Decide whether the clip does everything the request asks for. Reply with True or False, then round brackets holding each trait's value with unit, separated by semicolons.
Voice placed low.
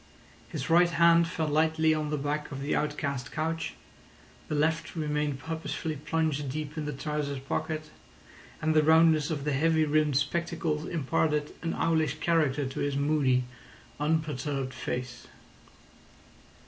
False (150 Hz)